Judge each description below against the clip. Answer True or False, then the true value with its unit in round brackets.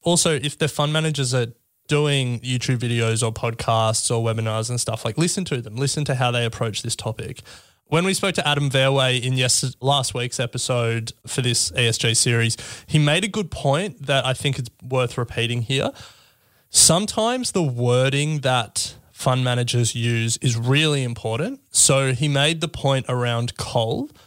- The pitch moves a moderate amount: True (3.4 semitones)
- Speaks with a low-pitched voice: True (125 Hz)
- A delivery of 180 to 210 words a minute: False (170 wpm)